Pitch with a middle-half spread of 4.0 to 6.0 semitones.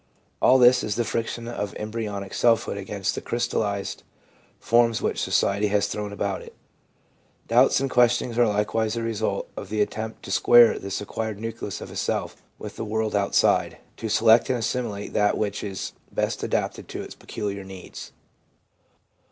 No: narrow, 2.4 semitones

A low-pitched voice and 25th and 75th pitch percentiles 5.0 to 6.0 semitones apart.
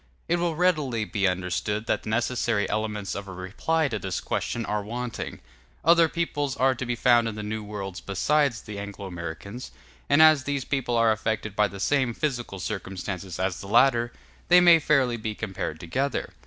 Yes: low, 115 Hz; average, 5.3 semitones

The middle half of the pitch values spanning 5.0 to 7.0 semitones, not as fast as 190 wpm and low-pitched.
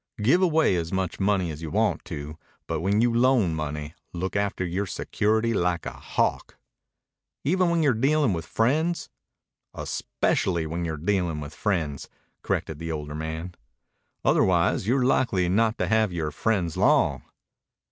Yes: wide, 5.6 semitones; average, 155 wpm; very low, 95 Hz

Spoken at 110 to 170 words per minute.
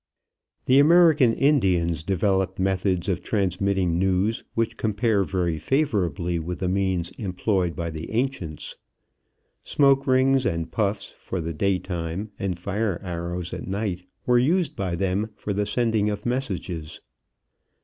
Yes: slow, 135 wpm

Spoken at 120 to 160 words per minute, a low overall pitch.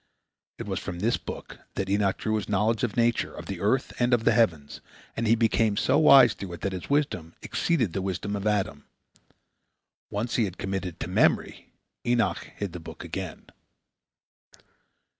No: average, 180 wpm; low, 105 Hz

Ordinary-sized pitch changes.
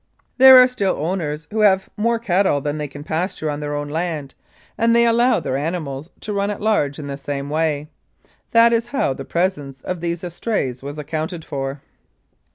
No: wide, 6.1 semitones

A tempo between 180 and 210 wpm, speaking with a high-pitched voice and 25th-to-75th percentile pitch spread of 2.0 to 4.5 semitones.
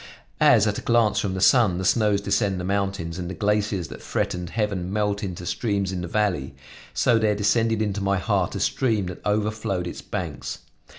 No: average, 195 wpm; low, 100 Hz; average, 2.7 semitones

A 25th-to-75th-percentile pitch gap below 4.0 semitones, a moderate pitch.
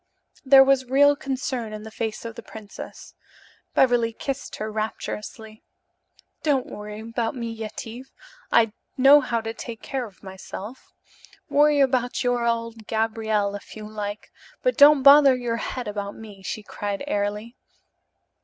No: average, 3.5 semitones; high, 230 Hz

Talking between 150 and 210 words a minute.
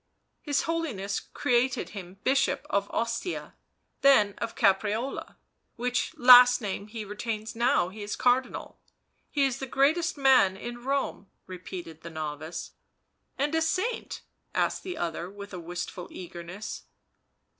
No: slow, 135 wpm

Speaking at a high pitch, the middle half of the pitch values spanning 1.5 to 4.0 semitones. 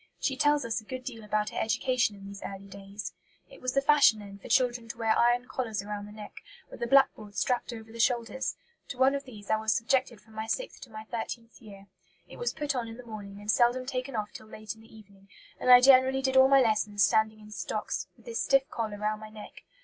Yes: high, 225 Hz; average, 3.3 semitones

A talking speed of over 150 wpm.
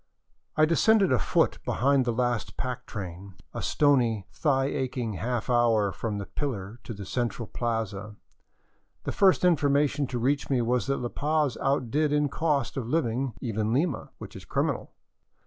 Yes: average, 160 wpm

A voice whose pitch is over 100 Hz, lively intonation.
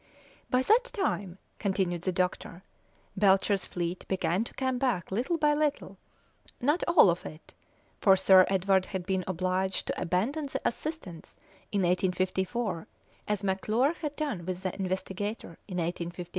No: high, 190 Hz; average, 5.0 semitones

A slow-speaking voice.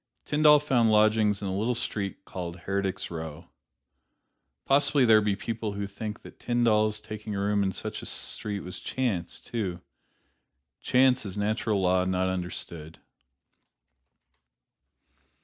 Yes: slow, 130 wpm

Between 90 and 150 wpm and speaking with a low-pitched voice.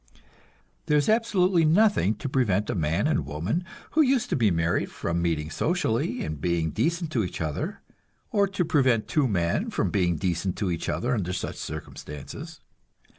No: average, 175 wpm; low, 110 Hz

